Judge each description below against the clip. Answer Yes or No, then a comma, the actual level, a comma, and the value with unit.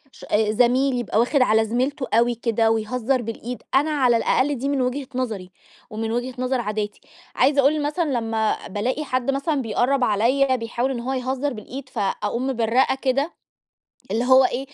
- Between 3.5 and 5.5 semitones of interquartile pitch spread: No, average, 3.1 semitones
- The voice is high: Yes, very high, 250 Hz